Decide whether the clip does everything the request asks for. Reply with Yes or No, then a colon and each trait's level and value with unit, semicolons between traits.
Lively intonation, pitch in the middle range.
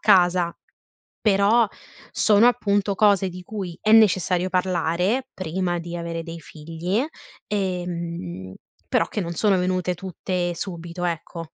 No: average, 2.8 semitones; medium, 180 Hz